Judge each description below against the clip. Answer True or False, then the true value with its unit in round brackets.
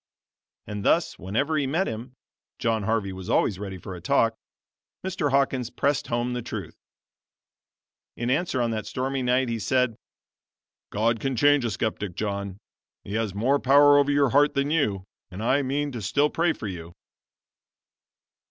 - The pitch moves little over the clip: False (5.3 semitones)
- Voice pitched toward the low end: True (120 Hz)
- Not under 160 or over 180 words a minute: True (165 wpm)